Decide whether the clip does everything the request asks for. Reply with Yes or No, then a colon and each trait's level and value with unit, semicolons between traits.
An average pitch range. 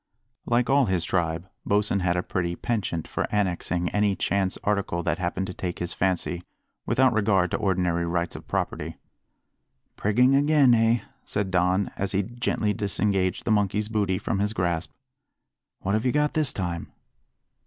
Yes: average, 3.5 semitones